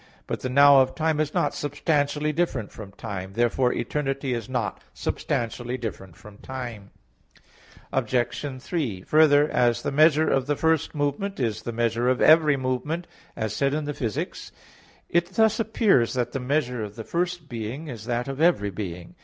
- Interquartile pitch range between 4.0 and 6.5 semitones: Yes, average, 4.5 semitones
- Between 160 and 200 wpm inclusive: Yes, average, 170 wpm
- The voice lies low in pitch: Yes, low, 130 Hz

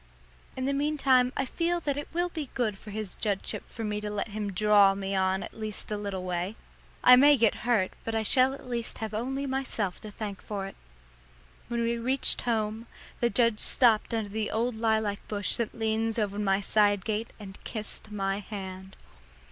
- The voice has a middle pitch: No, high, 220 Hz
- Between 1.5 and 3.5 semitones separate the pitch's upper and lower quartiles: Yes, average, 3.0 semitones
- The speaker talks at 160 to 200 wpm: Yes, average, 195 wpm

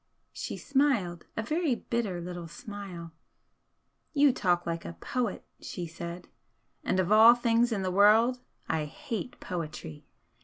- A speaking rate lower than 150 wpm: Yes, average, 140 wpm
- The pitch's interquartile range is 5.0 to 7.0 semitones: Yes, wide, 5.5 semitones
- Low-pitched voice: No, high, 200 Hz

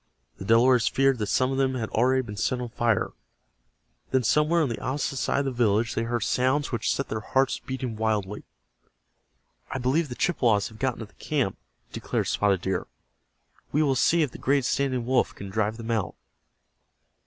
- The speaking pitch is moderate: No, low, 125 Hz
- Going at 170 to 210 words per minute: Yes, average, 190 wpm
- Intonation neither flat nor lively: Yes, average, 3.3 semitones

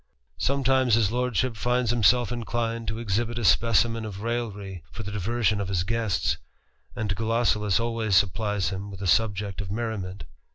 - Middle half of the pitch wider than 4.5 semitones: No, average, 2.8 semitones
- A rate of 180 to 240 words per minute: No, average, 160 wpm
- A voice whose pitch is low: Yes, low, 110 Hz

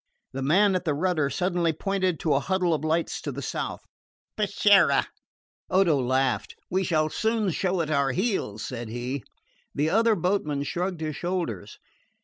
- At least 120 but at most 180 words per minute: Yes, average, 160 wpm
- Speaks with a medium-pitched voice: Yes, medium, 165 Hz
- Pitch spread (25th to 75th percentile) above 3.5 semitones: Yes, average, 5.1 semitones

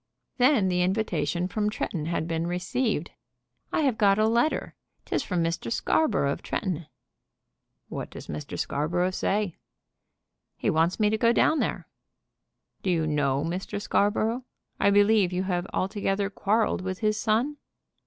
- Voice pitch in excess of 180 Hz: Yes, high, 190 Hz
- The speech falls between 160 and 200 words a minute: No, average, 150 wpm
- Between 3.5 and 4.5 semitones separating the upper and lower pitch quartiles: Yes, average, 4.1 semitones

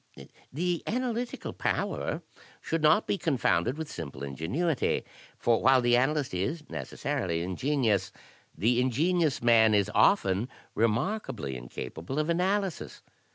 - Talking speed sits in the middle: No, slow, 120 wpm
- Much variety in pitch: Yes, wide, 8.2 semitones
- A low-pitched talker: Yes, low, 130 Hz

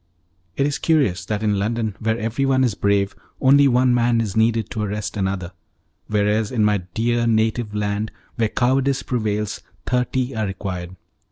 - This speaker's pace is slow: No, average, 160 wpm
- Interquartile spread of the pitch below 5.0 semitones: Yes, average, 3.1 semitones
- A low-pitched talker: Yes, low, 110 Hz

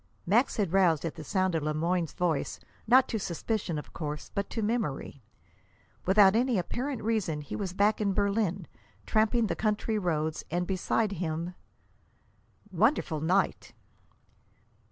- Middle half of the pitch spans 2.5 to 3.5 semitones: No, average, 4.7 semitones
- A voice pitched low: No, high, 190 Hz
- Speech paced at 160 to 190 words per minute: No, average, 145 wpm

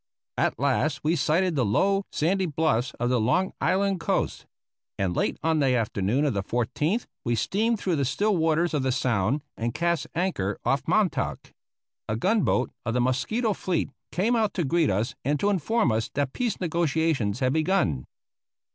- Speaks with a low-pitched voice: No, medium, 150 Hz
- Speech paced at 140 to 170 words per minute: No, average, 180 wpm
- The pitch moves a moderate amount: No, wide, 7.1 semitones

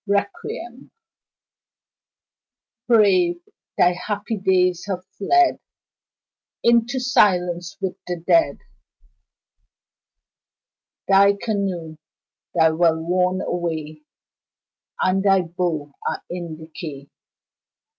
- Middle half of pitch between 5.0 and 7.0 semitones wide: No, average, 3.0 semitones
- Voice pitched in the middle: Yes, medium, 180 Hz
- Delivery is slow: Yes, slow, 80 wpm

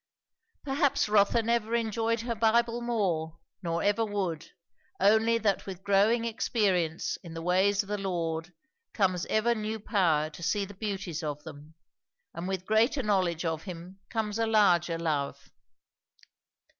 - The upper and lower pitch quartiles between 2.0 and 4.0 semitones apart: No, average, 4.5 semitones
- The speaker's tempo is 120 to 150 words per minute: Yes, average, 145 wpm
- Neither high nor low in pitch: No, high, 200 Hz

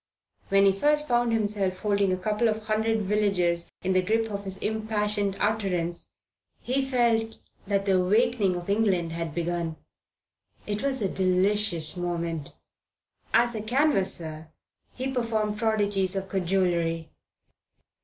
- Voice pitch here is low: No, high, 200 Hz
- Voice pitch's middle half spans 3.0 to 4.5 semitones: Yes, average, 3.4 semitones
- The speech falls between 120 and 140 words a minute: Yes, slow, 135 wpm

